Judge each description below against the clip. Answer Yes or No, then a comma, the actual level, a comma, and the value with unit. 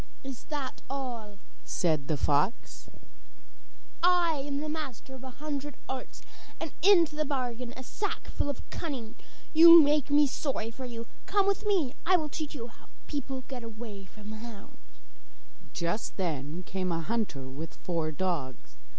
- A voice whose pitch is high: Yes, very high, 255 Hz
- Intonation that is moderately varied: No, wide, 6.9 semitones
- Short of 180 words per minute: Yes, average, 160 wpm